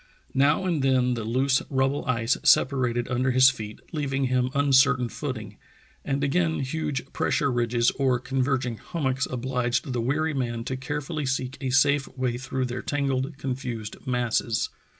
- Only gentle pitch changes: Yes, narrow, 2.0 semitones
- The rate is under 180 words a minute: Yes, average, 150 wpm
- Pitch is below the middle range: Yes, low, 130 Hz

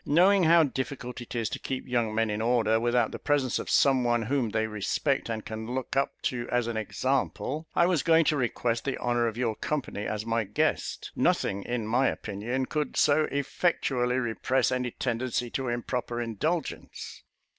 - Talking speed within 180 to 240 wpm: Yes, average, 185 wpm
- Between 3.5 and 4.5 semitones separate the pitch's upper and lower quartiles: No, average, 3.1 semitones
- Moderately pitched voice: No, low, 125 Hz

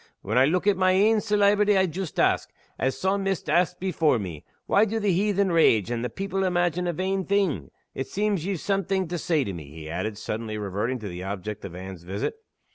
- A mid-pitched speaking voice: Yes, medium, 175 Hz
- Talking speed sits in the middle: No, fast, 215 wpm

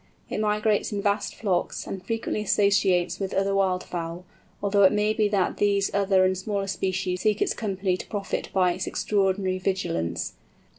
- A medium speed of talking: Yes, average, 170 wpm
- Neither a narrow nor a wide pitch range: No, narrow, 1.7 semitones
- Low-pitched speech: No, high, 195 Hz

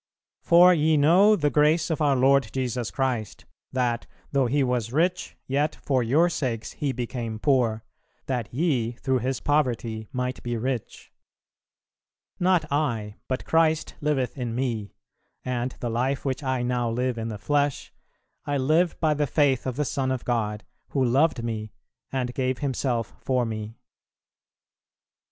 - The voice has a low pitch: Yes, low, 130 Hz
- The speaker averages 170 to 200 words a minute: No, average, 155 wpm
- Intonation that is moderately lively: Yes, average, 3.6 semitones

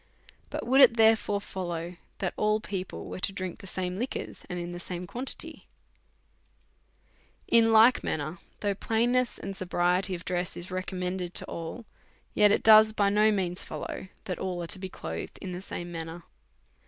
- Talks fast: No, average, 170 wpm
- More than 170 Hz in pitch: Yes, medium, 185 Hz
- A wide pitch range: No, average, 3.4 semitones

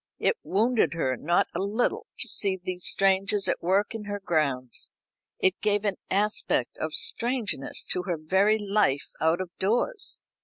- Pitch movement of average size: Yes, average, 3.3 semitones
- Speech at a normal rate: Yes, average, 160 wpm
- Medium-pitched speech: No, high, 195 Hz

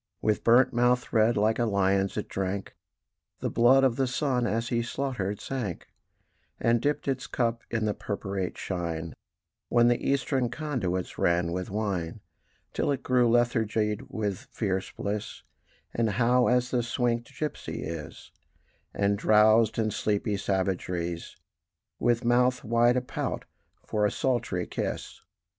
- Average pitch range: Yes, average, 3.7 semitones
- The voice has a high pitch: No, low, 115 Hz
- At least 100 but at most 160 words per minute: Yes, average, 145 wpm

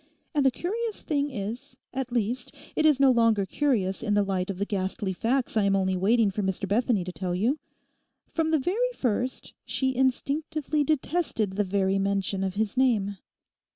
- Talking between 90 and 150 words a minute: No, average, 175 wpm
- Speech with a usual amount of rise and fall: No, wide, 5.8 semitones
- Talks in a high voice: Yes, high, 230 Hz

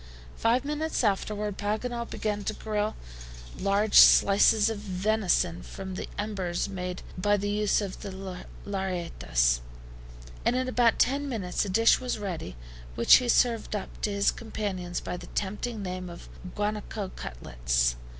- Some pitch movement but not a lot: Yes, average, 3.0 semitones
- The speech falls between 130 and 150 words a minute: Yes, average, 145 wpm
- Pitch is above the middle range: Yes, high, 205 Hz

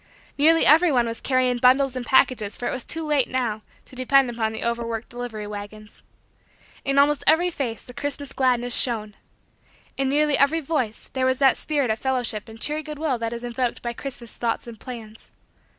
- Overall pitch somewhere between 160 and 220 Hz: No, very high, 250 Hz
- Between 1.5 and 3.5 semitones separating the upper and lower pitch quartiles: Yes, average, 3.2 semitones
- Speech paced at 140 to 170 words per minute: No, average, 190 wpm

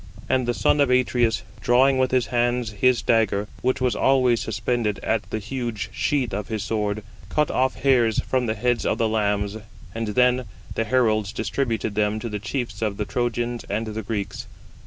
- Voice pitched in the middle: No, low, 115 Hz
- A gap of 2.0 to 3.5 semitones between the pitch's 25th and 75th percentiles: Yes, average, 2.7 semitones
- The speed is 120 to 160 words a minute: No, average, 185 wpm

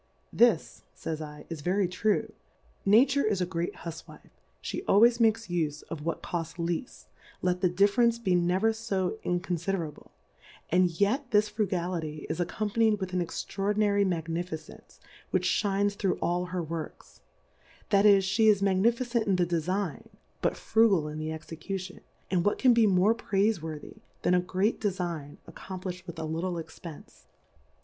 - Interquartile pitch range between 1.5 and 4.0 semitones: Yes, average, 3.6 semitones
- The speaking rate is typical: Yes, average, 160 wpm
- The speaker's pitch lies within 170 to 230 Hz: Yes, medium, 185 Hz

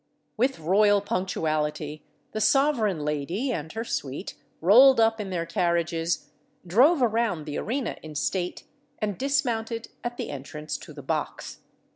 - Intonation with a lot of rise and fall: Yes, wide, 6.6 semitones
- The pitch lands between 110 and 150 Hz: No, high, 190 Hz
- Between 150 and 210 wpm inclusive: No, average, 140 wpm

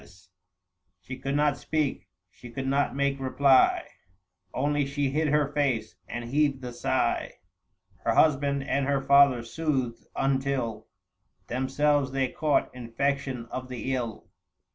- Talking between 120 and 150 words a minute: Yes, slow, 135 wpm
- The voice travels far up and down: No, narrow, 2.6 semitones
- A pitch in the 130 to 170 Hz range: Yes, low, 135 Hz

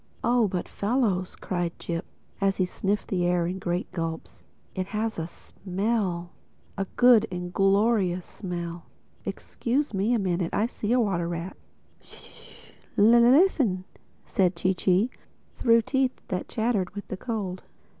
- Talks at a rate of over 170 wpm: No, slow, 135 wpm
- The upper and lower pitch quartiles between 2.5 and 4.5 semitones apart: Yes, average, 4.2 semitones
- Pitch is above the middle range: Yes, high, 195 Hz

